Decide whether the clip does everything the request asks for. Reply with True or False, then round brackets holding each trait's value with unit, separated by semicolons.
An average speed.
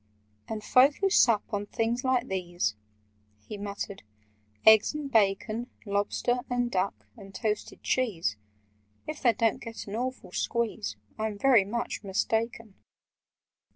False (120 wpm)